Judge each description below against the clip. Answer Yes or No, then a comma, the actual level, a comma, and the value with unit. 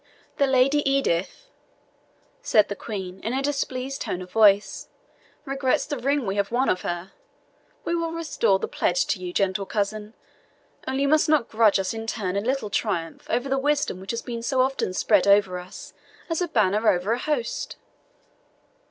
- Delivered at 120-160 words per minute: No, average, 180 wpm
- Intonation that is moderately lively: No, wide, 5.8 semitones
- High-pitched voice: Yes, high, 225 Hz